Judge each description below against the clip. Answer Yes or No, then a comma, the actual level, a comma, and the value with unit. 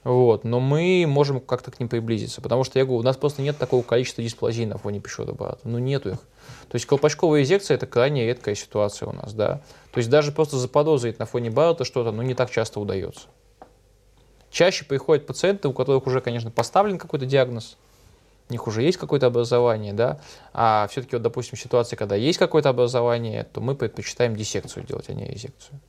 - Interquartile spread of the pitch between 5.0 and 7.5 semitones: No, average, 3.3 semitones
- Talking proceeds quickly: Yes, fast, 195 wpm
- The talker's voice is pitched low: Yes, low, 125 Hz